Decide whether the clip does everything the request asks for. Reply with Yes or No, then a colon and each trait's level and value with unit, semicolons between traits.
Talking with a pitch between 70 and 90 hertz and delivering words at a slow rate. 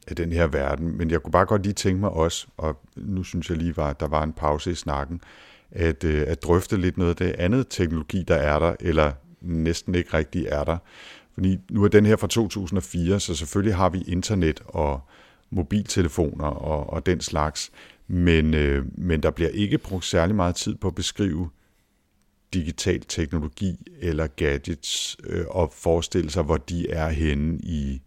No: very low, 85 Hz; average, 185 wpm